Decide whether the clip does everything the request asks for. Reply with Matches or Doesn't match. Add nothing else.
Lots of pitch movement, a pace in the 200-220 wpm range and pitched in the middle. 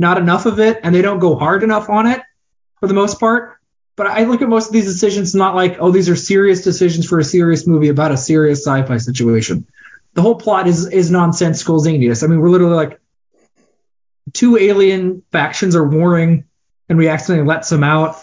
Doesn't match